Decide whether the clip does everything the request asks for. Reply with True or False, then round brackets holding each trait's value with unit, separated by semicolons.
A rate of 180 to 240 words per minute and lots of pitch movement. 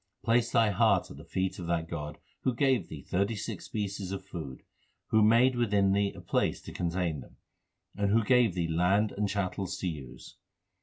False (195 wpm; 3.9 semitones)